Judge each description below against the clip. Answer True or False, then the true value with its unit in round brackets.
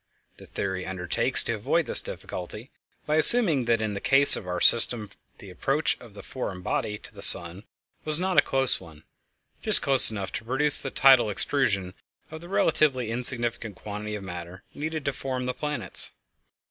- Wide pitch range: True (6.0 semitones)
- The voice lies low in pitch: True (115 Hz)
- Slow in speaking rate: False (175 wpm)